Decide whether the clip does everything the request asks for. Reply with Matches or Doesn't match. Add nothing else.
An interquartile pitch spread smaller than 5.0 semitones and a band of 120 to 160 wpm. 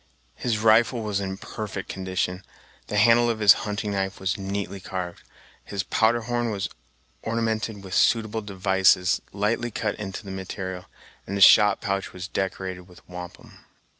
Matches